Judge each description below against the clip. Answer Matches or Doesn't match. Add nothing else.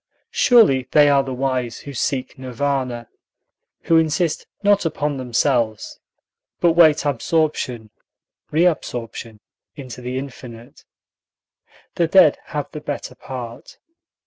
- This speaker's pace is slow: Matches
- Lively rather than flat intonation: Doesn't match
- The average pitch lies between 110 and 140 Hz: Matches